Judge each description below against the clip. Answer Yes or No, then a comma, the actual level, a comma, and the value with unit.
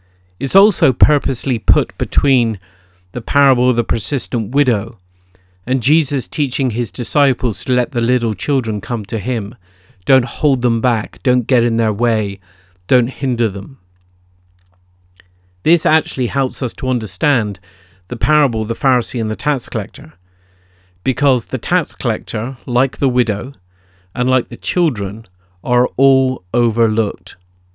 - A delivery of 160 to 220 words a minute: No, average, 140 wpm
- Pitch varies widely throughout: Yes, wide, 5.9 semitones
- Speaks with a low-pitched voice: Yes, low, 120 Hz